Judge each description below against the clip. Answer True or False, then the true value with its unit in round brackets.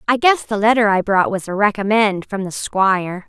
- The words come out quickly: True (220 wpm)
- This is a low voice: False (205 Hz)